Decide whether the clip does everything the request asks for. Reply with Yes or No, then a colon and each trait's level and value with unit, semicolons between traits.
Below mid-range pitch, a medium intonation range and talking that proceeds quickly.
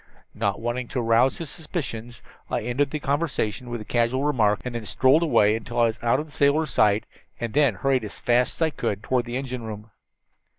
Yes: low, 120 Hz; average, 3.4 semitones; fast, 215 wpm